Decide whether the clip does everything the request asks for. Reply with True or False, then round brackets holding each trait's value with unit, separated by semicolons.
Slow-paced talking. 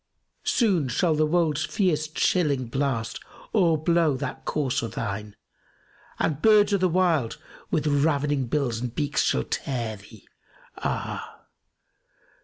True (130 wpm)